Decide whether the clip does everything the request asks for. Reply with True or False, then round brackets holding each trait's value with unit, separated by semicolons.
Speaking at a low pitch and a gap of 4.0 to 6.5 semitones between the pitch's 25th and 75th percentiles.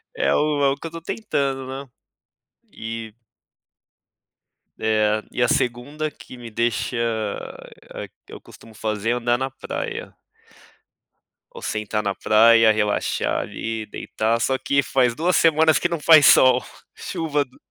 True (120 Hz; 4.3 semitones)